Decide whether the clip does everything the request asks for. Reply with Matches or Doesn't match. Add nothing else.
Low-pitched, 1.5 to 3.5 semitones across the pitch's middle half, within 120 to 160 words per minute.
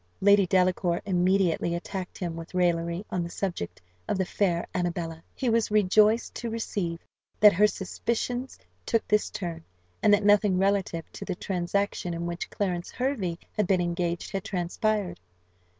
Doesn't match